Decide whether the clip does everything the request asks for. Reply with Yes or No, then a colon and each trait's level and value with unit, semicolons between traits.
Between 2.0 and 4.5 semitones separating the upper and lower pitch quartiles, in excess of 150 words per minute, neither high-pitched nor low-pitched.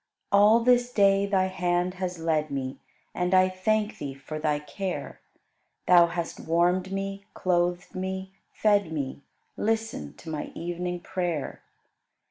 No: average, 2.8 semitones; slow, 135 wpm; medium, 180 Hz